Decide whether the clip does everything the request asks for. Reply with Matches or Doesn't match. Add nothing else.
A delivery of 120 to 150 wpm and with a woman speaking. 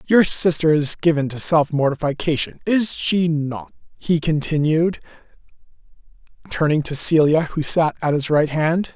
Doesn't match